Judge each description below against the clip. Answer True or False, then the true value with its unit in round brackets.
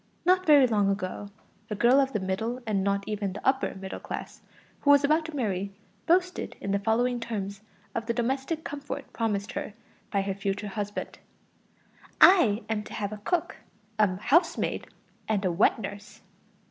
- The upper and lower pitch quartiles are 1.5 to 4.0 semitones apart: False (5.1 semitones)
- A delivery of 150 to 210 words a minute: True (170 wpm)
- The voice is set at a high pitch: True (215 Hz)